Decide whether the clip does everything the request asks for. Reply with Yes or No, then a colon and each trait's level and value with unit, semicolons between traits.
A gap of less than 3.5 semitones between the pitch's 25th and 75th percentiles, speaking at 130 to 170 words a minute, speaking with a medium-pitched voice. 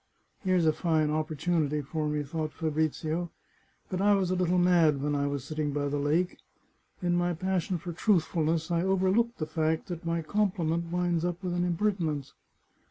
No: narrow, 2.6 semitones; average, 185 wpm; medium, 165 Hz